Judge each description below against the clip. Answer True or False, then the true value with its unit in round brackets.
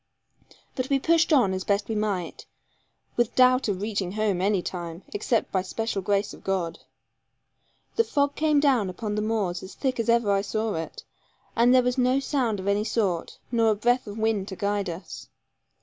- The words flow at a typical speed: True (195 wpm)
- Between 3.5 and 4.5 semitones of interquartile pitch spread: True (4.1 semitones)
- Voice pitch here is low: False (215 Hz)